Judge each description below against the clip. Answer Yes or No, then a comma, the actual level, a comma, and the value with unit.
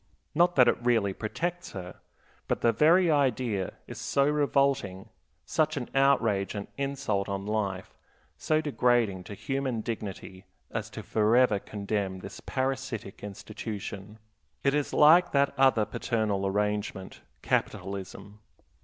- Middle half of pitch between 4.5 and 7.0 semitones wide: Yes, wide, 5.5 semitones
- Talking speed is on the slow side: Yes, slow, 125 wpm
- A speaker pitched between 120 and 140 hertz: No, low, 110 Hz